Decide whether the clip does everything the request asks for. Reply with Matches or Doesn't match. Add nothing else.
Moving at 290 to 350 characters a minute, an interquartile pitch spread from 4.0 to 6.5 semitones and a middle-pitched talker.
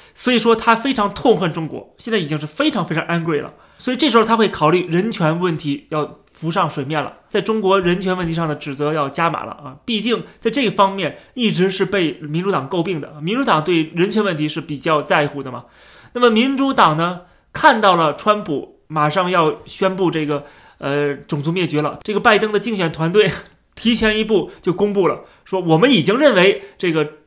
Matches